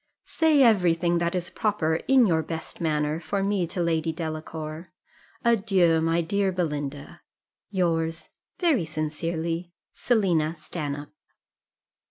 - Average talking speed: No, slow, 120 wpm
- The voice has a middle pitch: Yes, medium, 170 Hz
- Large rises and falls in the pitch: No, average, 3.1 semitones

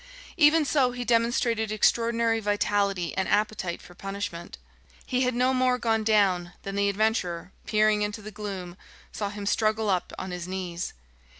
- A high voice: Yes, high, 210 Hz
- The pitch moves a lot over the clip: No, average, 3.3 semitones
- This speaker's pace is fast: No, average, 160 wpm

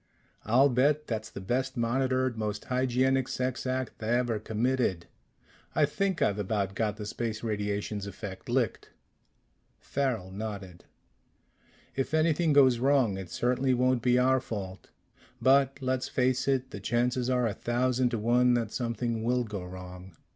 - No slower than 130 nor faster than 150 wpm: Yes, average, 145 wpm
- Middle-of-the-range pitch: No, low, 120 Hz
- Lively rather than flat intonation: No, average, 3.6 semitones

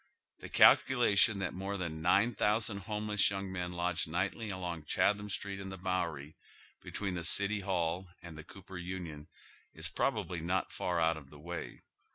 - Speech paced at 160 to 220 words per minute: Yes, average, 175 wpm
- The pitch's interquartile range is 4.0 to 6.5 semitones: No, average, 2.8 semitones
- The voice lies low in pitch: Yes, very low, 95 Hz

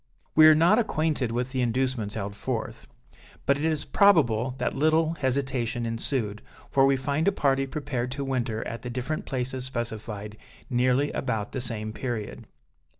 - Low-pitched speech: Yes, low, 130 Hz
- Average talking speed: Yes, average, 160 wpm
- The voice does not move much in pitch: No, average, 3.6 semitones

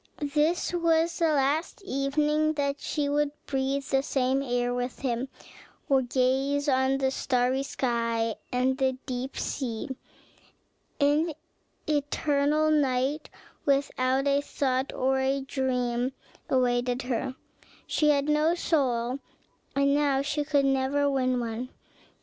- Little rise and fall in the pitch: Yes, narrow, 2.1 semitones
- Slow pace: Yes, slow, 125 wpm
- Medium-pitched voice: No, very high, 270 Hz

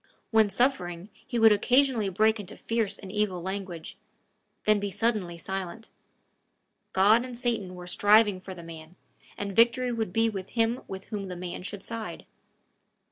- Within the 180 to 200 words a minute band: No, average, 160 wpm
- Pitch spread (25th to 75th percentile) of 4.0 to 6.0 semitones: No, average, 3.4 semitones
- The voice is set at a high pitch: Yes, high, 205 Hz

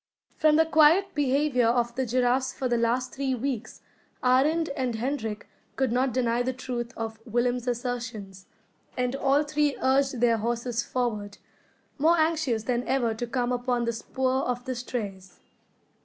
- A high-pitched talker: Yes, very high, 250 Hz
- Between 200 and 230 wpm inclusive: No, average, 155 wpm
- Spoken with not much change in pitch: Yes, narrow, 2.3 semitones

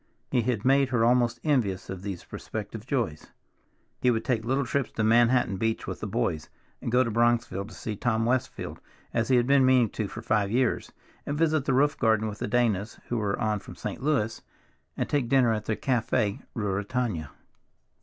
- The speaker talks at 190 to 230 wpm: Yes, average, 195 wpm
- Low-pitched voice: Yes, low, 115 Hz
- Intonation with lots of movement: No, average, 3.2 semitones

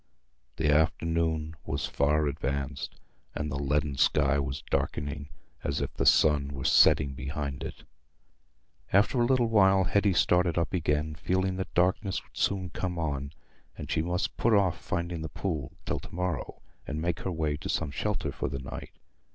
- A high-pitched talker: No, very low, 80 Hz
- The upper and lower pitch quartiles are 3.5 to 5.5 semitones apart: Yes, average, 4.0 semitones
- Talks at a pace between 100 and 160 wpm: No, average, 170 wpm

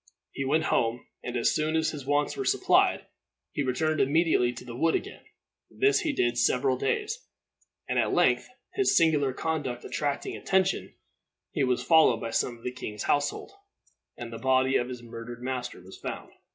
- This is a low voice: Yes, low, 130 Hz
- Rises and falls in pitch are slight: No, average, 4.6 semitones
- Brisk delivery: No, average, 180 wpm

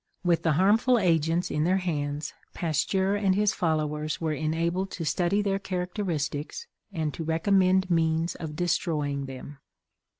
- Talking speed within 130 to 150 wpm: Yes, average, 140 wpm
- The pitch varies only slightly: No, average, 3.6 semitones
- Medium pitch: Yes, medium, 170 Hz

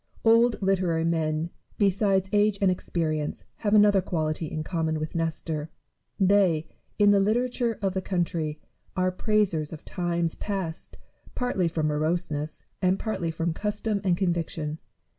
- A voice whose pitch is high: No, medium, 175 Hz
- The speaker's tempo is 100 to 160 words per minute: Yes, average, 140 wpm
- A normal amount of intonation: Yes, average, 4.0 semitones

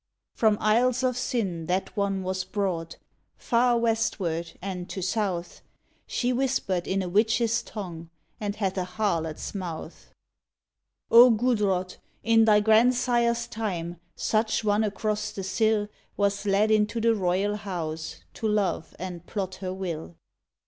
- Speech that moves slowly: No, average, 145 wpm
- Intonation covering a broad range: No, average, 3.5 semitones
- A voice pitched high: Yes, high, 205 Hz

